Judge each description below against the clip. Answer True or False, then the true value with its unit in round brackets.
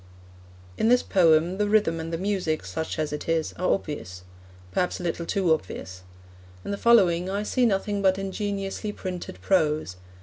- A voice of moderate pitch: True (180 Hz)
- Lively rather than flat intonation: False (4.1 semitones)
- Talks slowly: False (170 wpm)